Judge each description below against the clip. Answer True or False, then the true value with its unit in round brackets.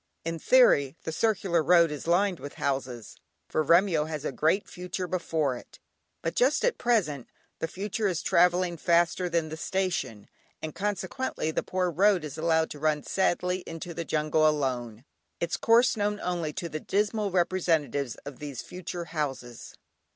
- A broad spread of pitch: False (3.5 semitones)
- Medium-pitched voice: True (170 Hz)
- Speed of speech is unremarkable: True (165 wpm)